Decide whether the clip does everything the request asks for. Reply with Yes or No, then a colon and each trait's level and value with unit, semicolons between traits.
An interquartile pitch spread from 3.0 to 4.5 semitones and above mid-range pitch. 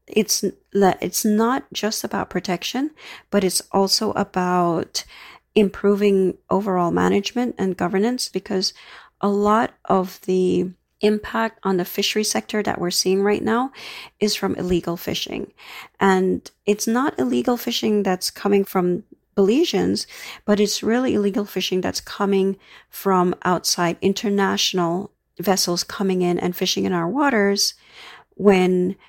No: narrow, 2.4 semitones; high, 195 Hz